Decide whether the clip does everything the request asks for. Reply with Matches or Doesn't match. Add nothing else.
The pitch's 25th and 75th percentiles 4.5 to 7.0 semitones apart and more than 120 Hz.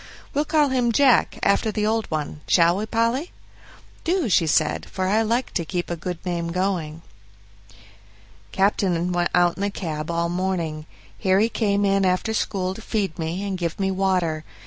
Doesn't match